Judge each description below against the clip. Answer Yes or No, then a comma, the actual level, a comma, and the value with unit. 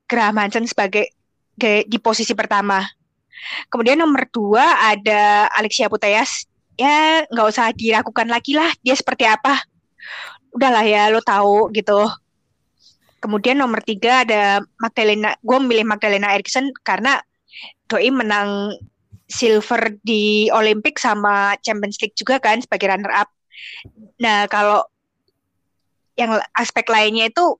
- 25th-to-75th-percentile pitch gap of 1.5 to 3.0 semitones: Yes, narrow, 2.5 semitones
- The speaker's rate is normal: Yes, average, 120 wpm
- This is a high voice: Yes, high, 220 Hz